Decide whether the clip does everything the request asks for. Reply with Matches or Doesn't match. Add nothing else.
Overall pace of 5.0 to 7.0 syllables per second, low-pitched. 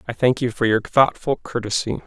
Matches